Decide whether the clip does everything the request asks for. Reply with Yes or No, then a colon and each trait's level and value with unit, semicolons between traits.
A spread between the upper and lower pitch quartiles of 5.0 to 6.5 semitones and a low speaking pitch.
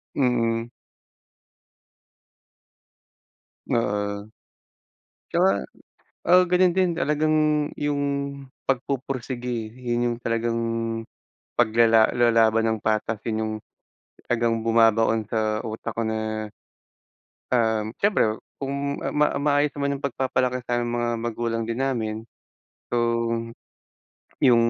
No: average, 3.1 semitones; low, 115 Hz